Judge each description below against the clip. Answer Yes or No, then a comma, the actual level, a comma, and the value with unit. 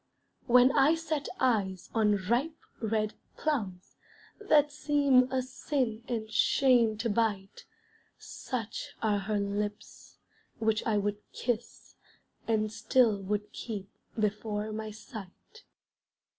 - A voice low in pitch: No, high, 220 Hz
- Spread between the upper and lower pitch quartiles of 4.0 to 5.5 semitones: No, average, 3.6 semitones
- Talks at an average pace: No, slow, 115 wpm